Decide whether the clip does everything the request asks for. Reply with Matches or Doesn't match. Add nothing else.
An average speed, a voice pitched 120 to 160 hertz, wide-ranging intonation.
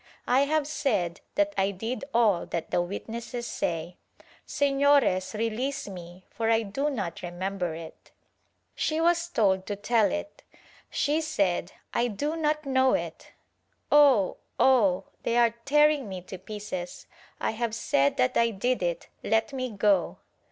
Doesn't match